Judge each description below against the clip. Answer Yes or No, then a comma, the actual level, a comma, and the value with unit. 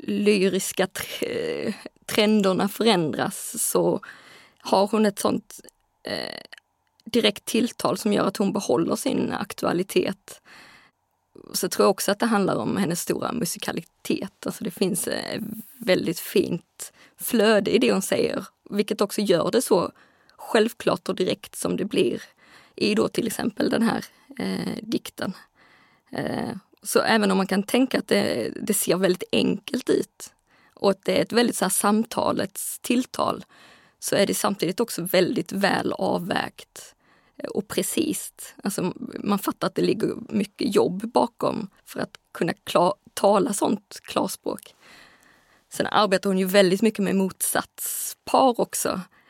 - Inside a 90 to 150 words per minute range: Yes, average, 145 wpm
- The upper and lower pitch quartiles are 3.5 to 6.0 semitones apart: No, average, 3.0 semitones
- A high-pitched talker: Yes, high, 210 Hz